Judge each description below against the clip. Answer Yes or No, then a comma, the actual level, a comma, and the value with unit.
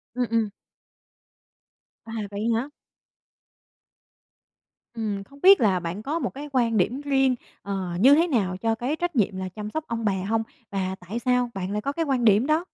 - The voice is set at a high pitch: Yes, high, 230 Hz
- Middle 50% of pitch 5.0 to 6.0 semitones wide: Yes, wide, 5.4 semitones